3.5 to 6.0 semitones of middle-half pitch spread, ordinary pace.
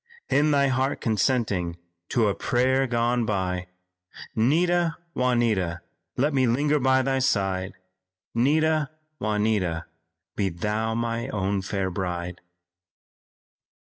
No: wide, 5.4 semitones; slow, 110 wpm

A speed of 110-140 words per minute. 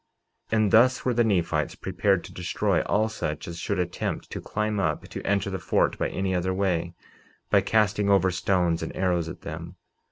No: average, 195 wpm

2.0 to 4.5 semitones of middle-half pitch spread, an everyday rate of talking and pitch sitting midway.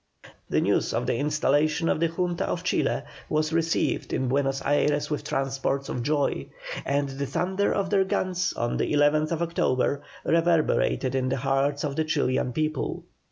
Yes: average, 3.2 semitones; average, 165 wpm; medium, 145 Hz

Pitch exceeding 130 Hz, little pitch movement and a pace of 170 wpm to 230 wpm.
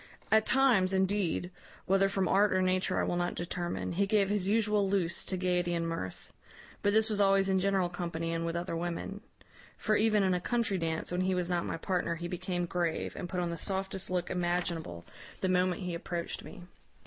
Yes: medium, 185 Hz; narrow, 2.1 semitones; fast, 205 wpm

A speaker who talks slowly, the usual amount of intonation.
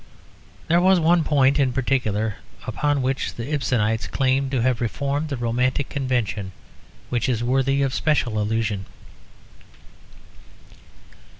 Yes: slow, 120 wpm; average, 3.4 semitones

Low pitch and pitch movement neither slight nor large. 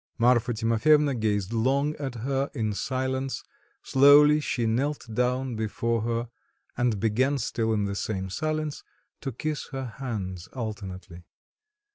Yes: low, 120 Hz; average, 3.8 semitones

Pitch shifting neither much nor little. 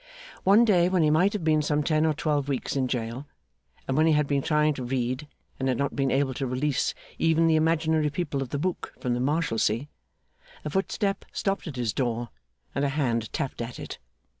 Yes: average, 3.5 semitones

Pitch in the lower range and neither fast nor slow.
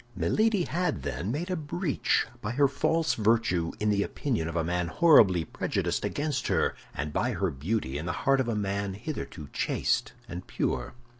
Yes: low, 110 Hz; average, 180 wpm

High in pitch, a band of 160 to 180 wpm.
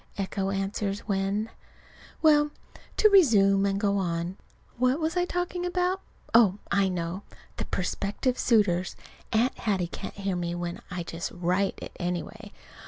No: high, 200 Hz; average, 145 wpm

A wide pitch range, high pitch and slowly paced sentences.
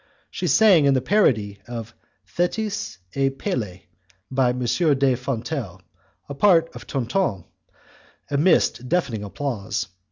No: wide, 6.3 semitones; low, 135 Hz; slow, 120 wpm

